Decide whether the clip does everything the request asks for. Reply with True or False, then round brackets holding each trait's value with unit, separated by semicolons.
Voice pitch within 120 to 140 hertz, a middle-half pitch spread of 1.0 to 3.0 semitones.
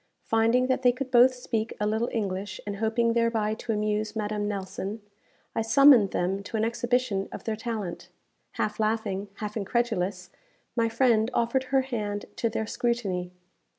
False (220 Hz; 2.4 semitones)